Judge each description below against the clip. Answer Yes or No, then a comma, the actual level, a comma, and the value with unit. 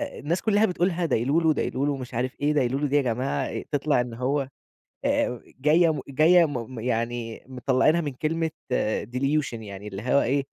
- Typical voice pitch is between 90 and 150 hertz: Yes, low, 135 Hz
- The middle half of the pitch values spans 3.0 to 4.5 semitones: Yes, average, 3.9 semitones